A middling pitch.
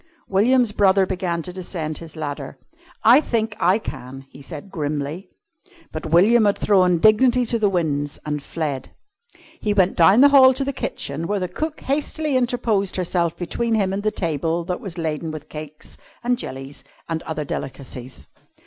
Yes: medium, 180 Hz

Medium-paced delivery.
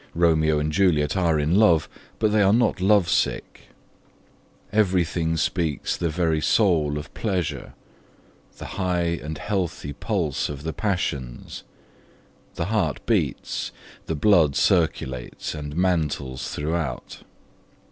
No: slow, 120 wpm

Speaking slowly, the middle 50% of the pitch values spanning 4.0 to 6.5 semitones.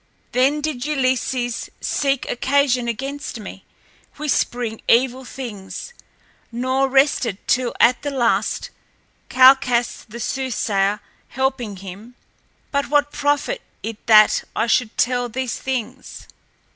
No: slow, 110 wpm; average, 2.7 semitones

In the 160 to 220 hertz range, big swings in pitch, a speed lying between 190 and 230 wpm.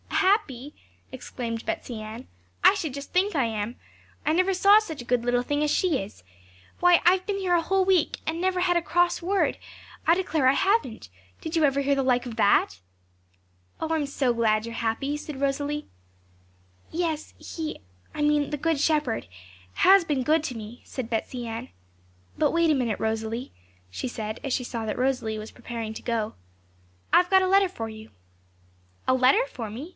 No: very high, 280 Hz; wide, 6.3 semitones; average, 195 wpm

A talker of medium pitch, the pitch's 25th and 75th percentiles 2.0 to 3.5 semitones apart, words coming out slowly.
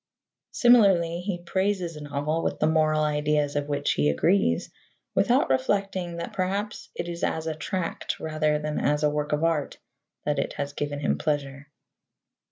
No: medium, 155 Hz; average, 2.9 semitones; average, 170 wpm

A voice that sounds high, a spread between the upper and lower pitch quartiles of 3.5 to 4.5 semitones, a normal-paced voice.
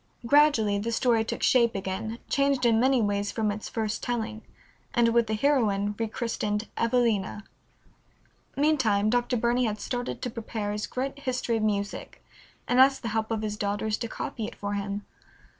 No: high, 225 Hz; average, 2.8 semitones; average, 170 wpm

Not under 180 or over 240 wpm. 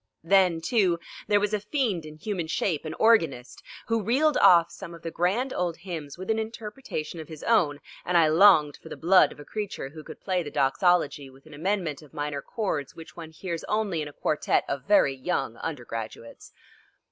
Yes: average, 200 wpm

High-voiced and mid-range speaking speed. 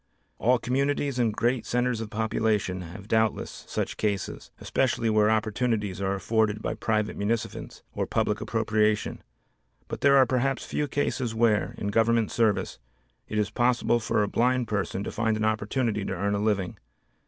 No: low, 110 Hz; average, 165 wpm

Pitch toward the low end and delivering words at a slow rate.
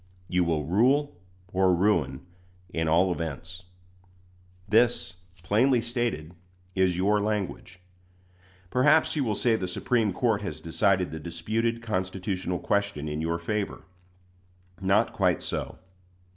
Yes: very low, 95 Hz; slow, 120 wpm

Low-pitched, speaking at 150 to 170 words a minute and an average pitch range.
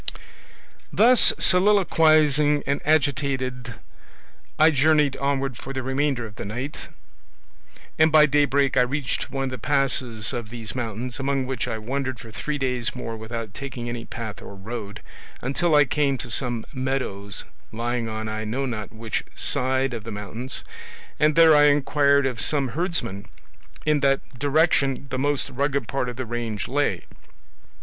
Yes: low, 130 Hz; average, 155 wpm; average, 3.6 semitones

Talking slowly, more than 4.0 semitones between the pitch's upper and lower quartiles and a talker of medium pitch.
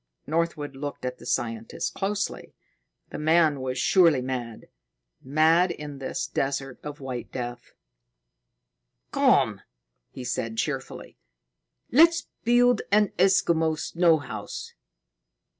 Yes: slow, 110 wpm; average, 4.9 semitones; medium, 150 Hz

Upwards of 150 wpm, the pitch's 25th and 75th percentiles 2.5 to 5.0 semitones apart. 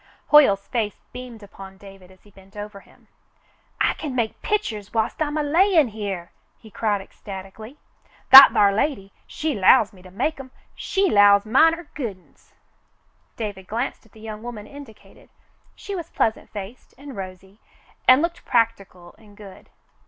No: average, 160 wpm; wide, 5.5 semitones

